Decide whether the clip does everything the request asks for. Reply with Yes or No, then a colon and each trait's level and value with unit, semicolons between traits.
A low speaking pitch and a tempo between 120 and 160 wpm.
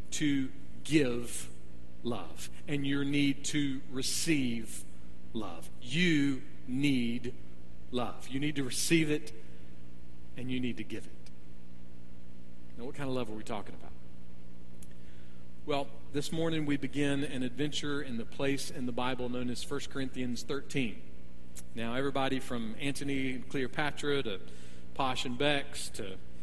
Yes: low, 125 Hz; average, 140 wpm